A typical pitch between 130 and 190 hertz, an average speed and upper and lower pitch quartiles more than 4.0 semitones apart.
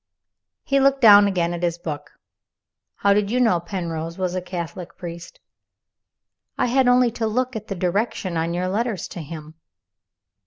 Yes: medium, 185 Hz; average, 165 wpm; average, 4.7 semitones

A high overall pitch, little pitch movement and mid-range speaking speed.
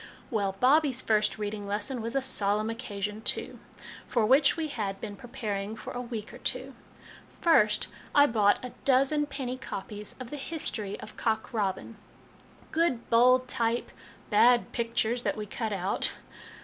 No: high, 230 Hz; average, 3.6 semitones; average, 160 wpm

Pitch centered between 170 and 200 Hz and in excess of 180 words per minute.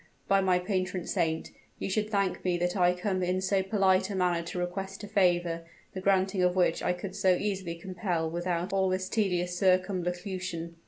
Yes: medium, 185 Hz; average, 190 wpm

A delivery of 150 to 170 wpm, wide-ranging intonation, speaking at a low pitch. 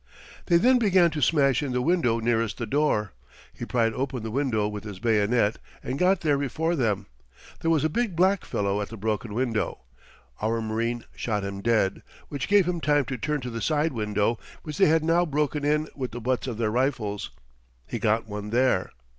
No: fast, 205 wpm; wide, 5.7 semitones; low, 125 Hz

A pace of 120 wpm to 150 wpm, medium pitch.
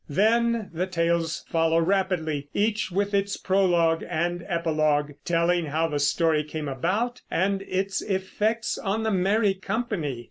Yes: average, 140 wpm; medium, 180 Hz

